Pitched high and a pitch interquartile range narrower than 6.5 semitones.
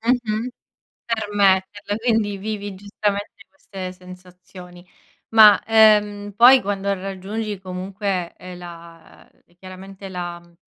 Yes: high, 195 Hz; narrow, 2.4 semitones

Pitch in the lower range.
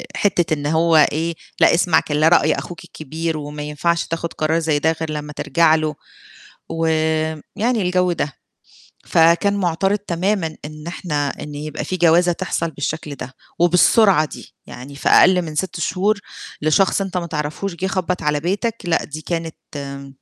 No: medium, 165 Hz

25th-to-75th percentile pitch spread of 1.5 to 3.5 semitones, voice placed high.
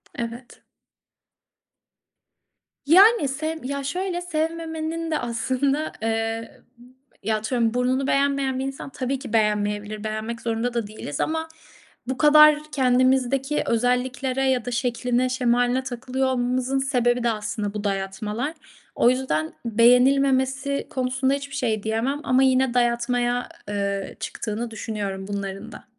Yes: average, 3.2 semitones; very high, 250 Hz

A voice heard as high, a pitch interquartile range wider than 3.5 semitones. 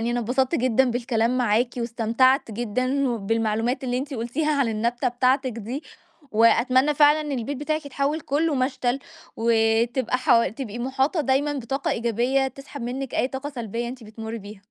No: very high, 250 Hz; average, 2.8 semitones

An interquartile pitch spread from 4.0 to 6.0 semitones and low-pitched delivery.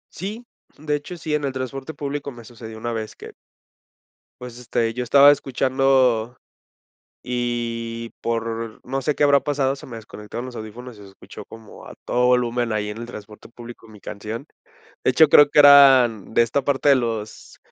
No: average, 3.3 semitones; low, 120 Hz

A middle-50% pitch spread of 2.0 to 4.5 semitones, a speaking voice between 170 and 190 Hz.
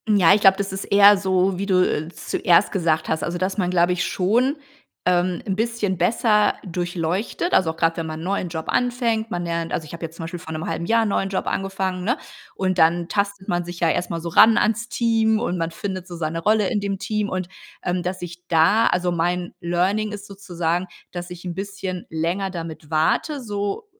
Yes: average, 2.9 semitones; medium, 185 Hz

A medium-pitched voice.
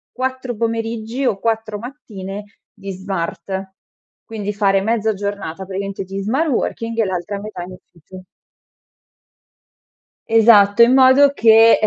No: high, 210 Hz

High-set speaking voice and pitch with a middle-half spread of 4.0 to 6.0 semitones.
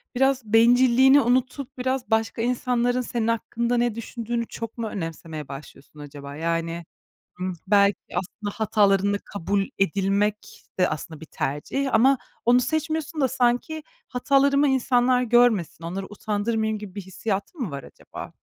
Yes: high, 225 Hz; average, 4.4 semitones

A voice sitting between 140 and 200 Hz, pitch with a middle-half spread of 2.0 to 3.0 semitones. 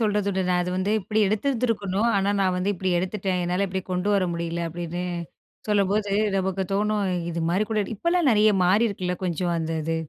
Yes: high, 190 Hz; average, 2.7 semitones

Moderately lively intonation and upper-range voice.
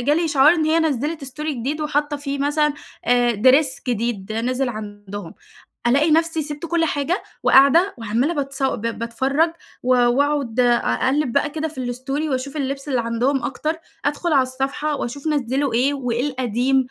Yes: average, 3.4 semitones; very high, 275 Hz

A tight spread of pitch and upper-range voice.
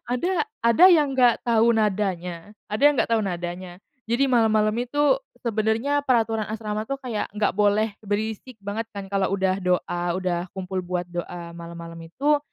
No: average, 4.2 semitones; high, 210 Hz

